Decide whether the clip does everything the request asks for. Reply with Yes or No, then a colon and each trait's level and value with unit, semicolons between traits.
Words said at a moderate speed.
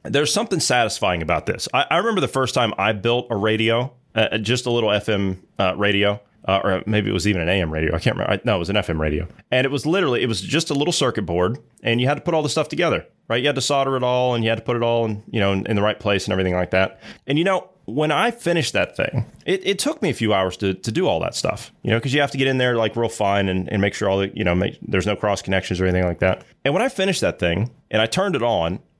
No: fast, 305 wpm